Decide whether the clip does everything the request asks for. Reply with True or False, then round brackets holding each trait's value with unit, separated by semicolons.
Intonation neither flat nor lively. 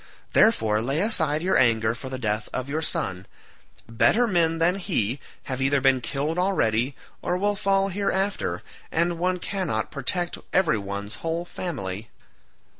False (8.1 semitones)